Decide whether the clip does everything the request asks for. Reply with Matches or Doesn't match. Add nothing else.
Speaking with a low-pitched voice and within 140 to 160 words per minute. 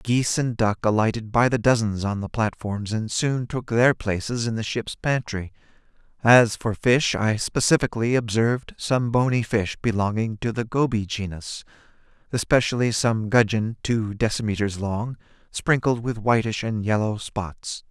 Matches